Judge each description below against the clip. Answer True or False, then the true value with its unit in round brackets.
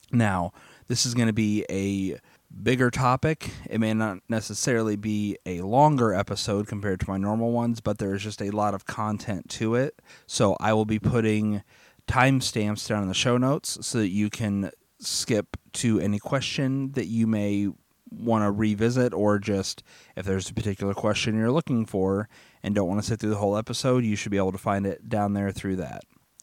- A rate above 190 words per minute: True (200 wpm)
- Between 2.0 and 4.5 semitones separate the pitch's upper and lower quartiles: True (2.7 semitones)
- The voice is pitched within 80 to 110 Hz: True (105 Hz)